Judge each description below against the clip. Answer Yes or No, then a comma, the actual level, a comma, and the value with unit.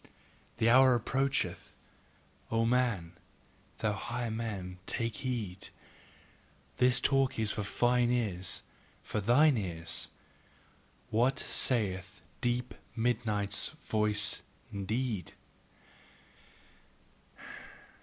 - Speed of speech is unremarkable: No, slow, 85 wpm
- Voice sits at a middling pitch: No, low, 115 Hz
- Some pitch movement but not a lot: Yes, average, 3.4 semitones